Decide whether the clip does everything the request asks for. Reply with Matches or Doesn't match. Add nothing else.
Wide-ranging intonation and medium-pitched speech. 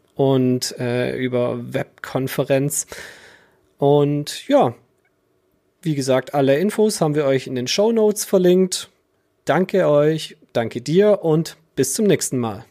Matches